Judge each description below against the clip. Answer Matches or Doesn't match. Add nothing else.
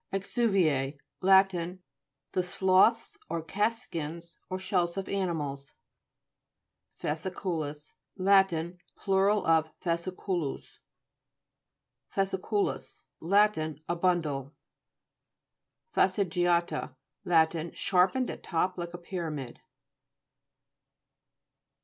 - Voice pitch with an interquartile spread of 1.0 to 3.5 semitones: Matches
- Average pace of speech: Doesn't match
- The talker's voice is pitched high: Doesn't match